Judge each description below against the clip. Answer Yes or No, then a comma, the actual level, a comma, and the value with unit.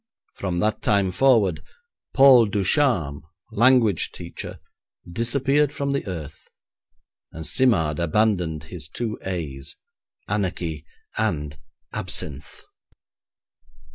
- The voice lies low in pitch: Yes, very low, 95 Hz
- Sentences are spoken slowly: Yes, slow, 90 wpm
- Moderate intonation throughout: No, wide, 6.8 semitones